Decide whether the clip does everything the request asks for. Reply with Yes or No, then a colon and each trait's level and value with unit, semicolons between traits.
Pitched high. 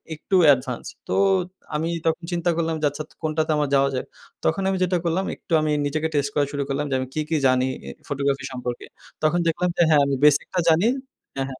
No: medium, 150 Hz